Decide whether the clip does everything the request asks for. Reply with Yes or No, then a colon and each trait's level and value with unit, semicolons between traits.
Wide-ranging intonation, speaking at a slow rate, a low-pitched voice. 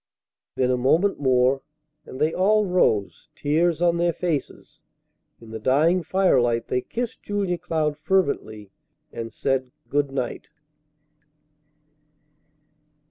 No: wide, 5.7 semitones; slow, 115 wpm; medium, 150 Hz